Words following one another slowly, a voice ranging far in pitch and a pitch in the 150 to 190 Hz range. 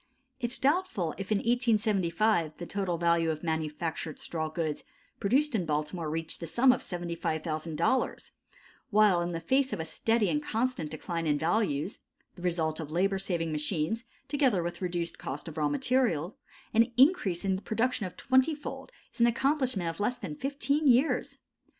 No: average, 170 wpm; wide, 6.8 semitones; medium, 185 Hz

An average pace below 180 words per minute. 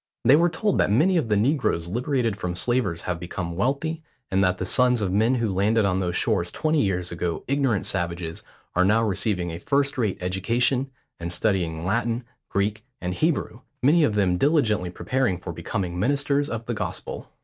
No: average, 185 wpm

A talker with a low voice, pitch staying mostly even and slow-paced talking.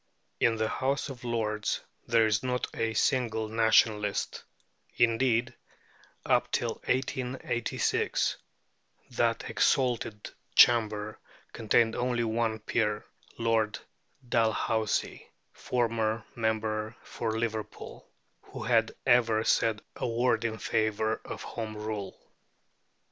Yes: low, 115 Hz; narrow, 1.5 semitones; slow, 100 wpm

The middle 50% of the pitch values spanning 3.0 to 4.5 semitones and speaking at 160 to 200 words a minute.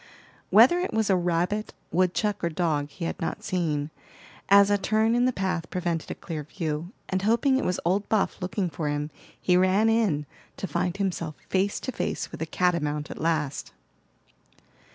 Yes: average, 3.9 semitones; average, 180 wpm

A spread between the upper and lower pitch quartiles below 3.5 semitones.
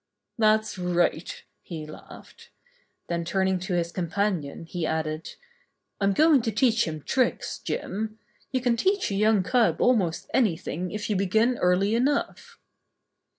No: average, 4.7 semitones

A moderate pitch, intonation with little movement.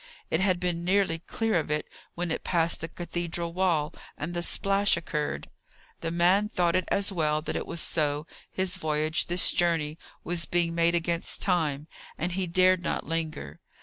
Yes: medium, 170 Hz; narrow, 2.1 semitones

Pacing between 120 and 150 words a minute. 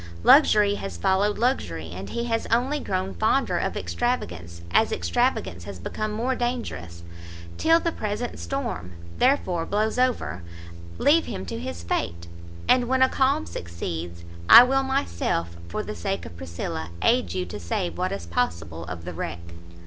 No: average, 160 wpm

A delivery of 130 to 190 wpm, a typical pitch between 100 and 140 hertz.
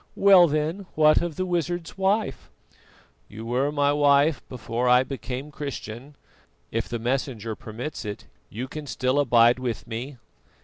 Yes: average, 145 wpm; low, 135 Hz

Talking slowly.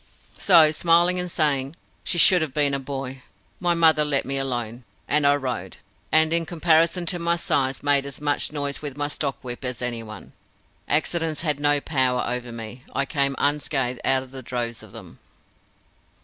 No: average, 180 wpm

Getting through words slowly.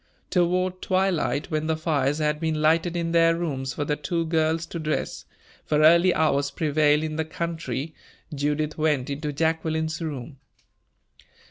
No: average, 150 wpm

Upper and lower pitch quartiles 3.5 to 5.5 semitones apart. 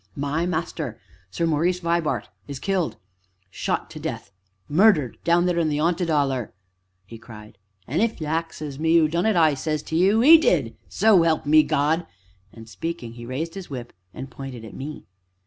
Yes: average, 4.1 semitones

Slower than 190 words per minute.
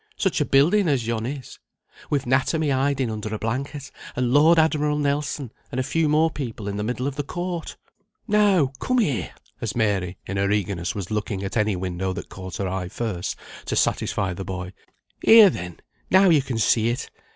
No: average, 195 wpm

